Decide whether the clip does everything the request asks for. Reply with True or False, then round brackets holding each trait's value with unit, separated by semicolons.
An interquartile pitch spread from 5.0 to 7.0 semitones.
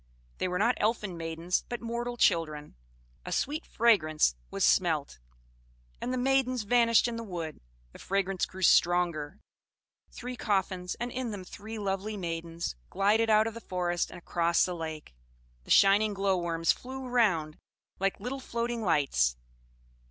True (5.4 semitones)